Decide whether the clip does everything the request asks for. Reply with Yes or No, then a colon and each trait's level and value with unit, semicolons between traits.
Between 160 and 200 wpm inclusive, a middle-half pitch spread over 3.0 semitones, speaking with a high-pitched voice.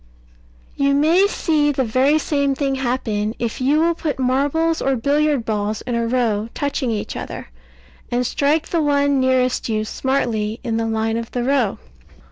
Yes: average, 170 wpm; average, 4.0 semitones; very high, 260 Hz